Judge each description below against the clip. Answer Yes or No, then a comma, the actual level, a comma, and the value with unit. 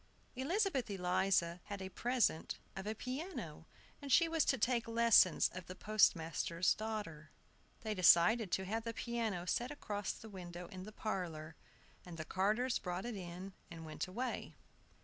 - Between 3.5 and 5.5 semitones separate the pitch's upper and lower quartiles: Yes, average, 4.7 semitones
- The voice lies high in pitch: Yes, high, 200 Hz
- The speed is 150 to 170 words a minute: Yes, average, 160 wpm